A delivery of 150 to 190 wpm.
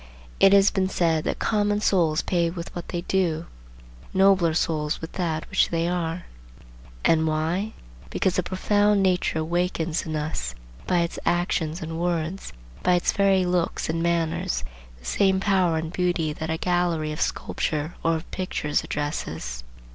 Yes: average, 160 wpm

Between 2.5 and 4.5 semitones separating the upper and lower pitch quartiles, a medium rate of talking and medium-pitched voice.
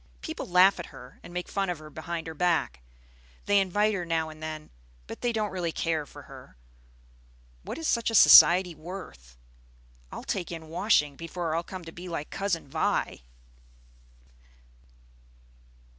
Yes: average, 3.3 semitones; average, 160 wpm; medium, 170 Hz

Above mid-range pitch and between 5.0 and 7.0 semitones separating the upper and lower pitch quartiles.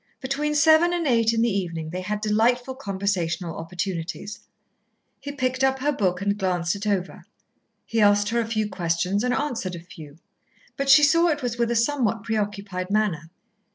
Yes: high, 210 Hz; wide, 5.5 semitones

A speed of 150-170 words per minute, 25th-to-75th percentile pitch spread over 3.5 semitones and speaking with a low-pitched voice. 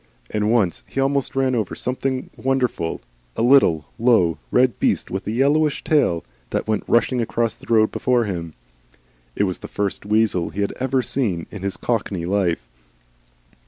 Yes: average, 165 wpm; average, 5.1 semitones; low, 110 Hz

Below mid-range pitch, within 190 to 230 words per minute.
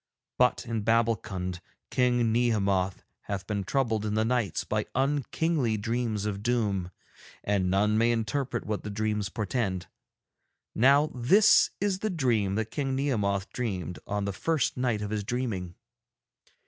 No: low, 110 Hz; average, 145 wpm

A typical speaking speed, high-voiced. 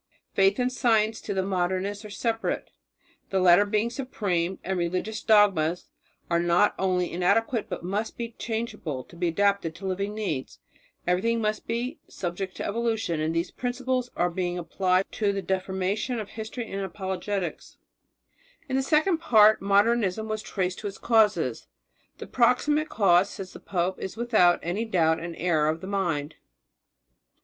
Yes: average, 160 wpm; high, 195 Hz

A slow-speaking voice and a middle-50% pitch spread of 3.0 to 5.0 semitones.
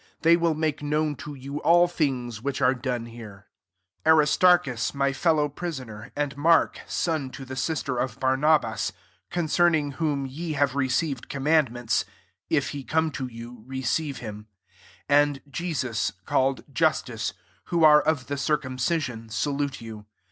No: average, 150 wpm; average, 3.8 semitones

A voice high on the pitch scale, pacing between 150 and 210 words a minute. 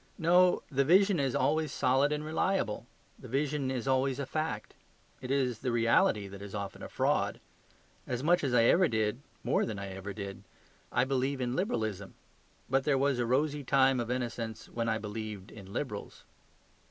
No: low, 130 Hz; average, 180 wpm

